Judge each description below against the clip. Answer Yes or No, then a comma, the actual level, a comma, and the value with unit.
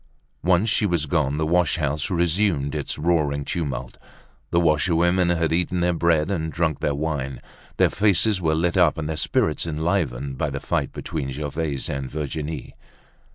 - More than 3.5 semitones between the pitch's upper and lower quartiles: No, average, 3.2 semitones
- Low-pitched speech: Yes, very low, 80 Hz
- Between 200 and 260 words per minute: No, average, 165 wpm